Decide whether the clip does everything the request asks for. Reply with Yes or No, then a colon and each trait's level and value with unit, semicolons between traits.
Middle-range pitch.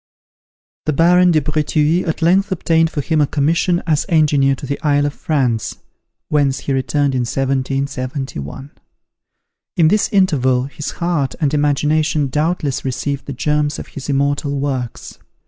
Yes: medium, 145 Hz